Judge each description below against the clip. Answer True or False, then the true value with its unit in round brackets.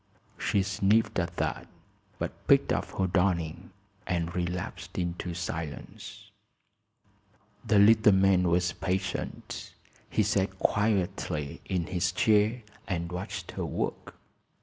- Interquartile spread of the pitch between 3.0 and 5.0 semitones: False (2.5 semitones)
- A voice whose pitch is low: True (90 Hz)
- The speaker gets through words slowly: True (115 wpm)